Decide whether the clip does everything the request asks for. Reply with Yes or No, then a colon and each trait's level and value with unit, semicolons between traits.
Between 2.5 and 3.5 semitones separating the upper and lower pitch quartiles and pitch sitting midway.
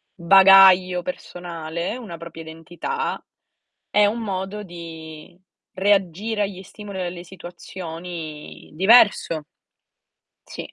Yes: average, 2.8 semitones; medium, 180 Hz